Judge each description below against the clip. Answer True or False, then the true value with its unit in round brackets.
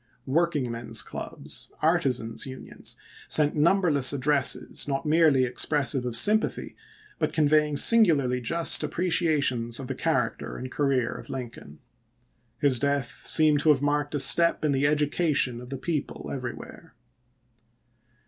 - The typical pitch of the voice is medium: True (145 Hz)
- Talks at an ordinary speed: False (130 wpm)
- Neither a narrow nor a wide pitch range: True (3.3 semitones)